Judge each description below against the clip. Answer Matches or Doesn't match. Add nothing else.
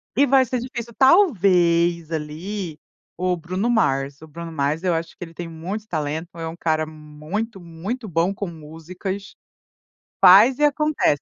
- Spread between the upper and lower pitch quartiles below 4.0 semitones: Doesn't match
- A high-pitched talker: Doesn't match